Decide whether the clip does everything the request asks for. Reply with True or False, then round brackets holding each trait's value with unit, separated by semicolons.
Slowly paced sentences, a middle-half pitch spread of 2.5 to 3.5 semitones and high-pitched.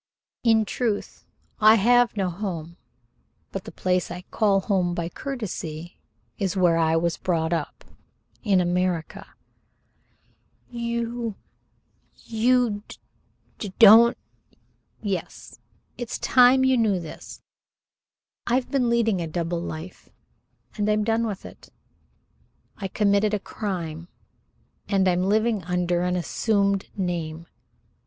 False (120 wpm; 4.3 semitones; 195 Hz)